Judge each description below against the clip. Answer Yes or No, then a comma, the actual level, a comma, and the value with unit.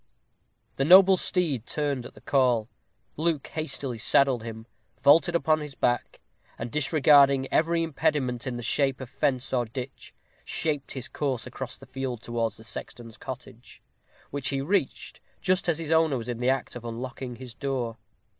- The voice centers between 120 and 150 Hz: Yes, low, 135 Hz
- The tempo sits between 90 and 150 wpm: No, average, 165 wpm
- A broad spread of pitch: No, average, 3.8 semitones